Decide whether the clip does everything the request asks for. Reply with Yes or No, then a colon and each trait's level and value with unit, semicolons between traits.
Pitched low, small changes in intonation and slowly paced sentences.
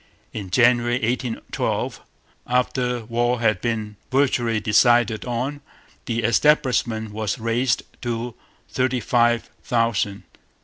Yes: low, 120 Hz; narrow, 1.9 semitones; slow, 100 wpm